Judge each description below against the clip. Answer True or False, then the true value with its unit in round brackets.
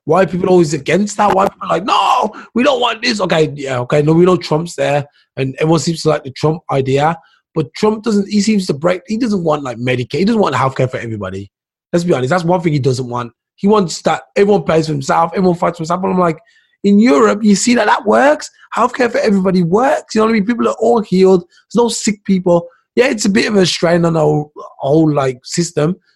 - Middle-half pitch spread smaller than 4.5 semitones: False (5.2 semitones)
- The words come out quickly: True (250 wpm)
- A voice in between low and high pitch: True (175 Hz)